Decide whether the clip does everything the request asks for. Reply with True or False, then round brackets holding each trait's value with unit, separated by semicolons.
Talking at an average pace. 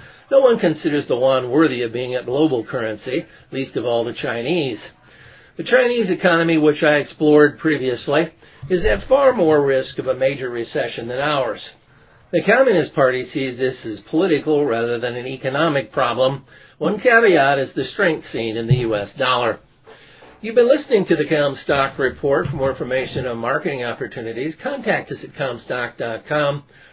True (165 wpm)